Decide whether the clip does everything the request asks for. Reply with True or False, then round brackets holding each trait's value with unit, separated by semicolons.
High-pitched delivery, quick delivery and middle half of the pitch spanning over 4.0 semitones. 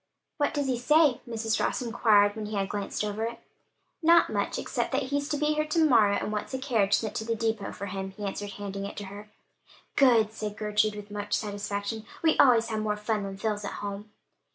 False (215 Hz; 225 wpm; 3.0 semitones)